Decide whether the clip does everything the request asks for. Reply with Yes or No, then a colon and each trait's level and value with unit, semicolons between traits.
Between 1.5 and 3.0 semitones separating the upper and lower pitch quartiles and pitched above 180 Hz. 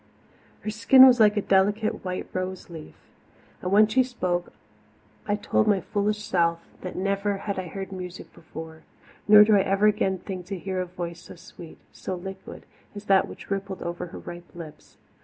Yes: narrow, 2.6 semitones; high, 190 Hz